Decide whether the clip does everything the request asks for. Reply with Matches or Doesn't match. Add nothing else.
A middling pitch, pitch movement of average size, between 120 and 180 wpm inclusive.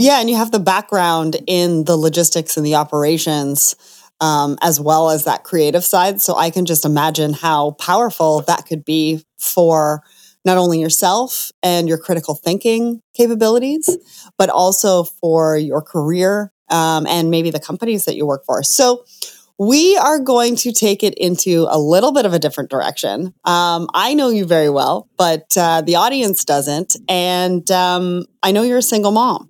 Matches